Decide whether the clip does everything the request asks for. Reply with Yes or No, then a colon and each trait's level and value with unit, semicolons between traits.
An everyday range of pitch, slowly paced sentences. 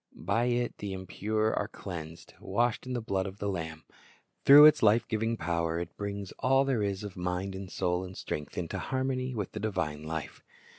No: average, 4.5 semitones; average, 195 wpm